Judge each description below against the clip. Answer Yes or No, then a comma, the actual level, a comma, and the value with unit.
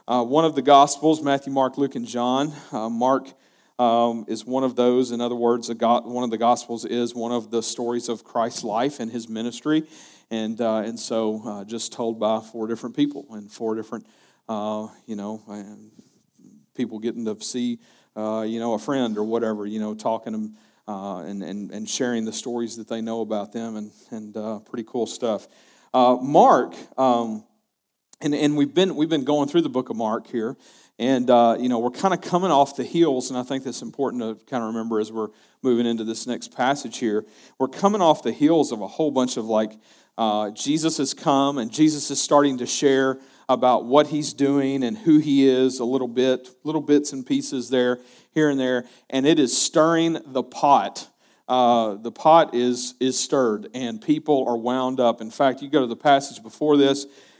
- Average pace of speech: No, fast, 210 wpm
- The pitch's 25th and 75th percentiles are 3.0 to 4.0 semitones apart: Yes, average, 3.6 semitones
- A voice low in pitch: Yes, low, 125 Hz